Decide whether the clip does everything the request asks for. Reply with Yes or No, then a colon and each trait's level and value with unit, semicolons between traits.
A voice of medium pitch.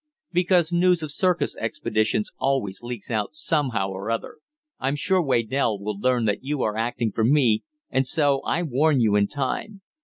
No: low, 130 Hz